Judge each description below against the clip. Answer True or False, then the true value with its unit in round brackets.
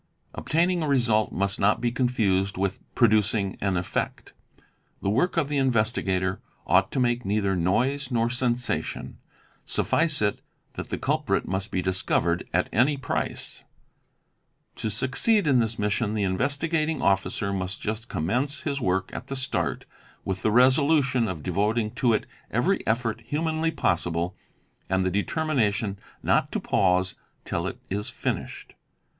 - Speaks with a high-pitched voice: False (110 Hz)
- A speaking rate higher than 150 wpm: False (145 wpm)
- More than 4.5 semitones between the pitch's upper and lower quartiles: True (5.4 semitones)